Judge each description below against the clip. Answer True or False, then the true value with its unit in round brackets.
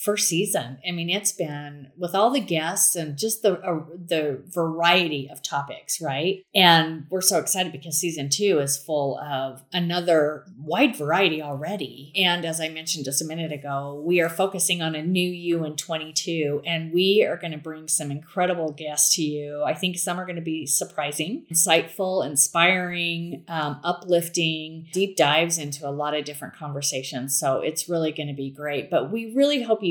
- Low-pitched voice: False (165 Hz)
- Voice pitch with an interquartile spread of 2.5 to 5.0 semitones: True (3.3 semitones)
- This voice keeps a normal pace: True (185 wpm)